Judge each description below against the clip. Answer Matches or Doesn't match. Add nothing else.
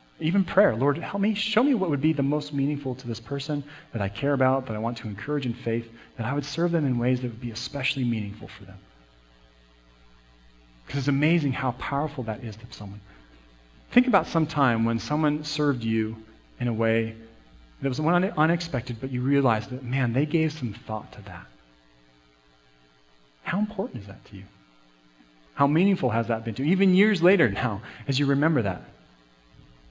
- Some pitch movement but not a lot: Doesn't match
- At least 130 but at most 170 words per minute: Doesn't match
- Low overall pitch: Matches